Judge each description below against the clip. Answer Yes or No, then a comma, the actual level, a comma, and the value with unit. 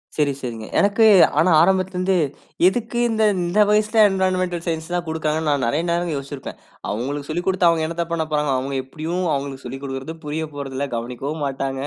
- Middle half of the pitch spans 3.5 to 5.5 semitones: Yes, average, 4.7 semitones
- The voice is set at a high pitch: No, medium, 160 Hz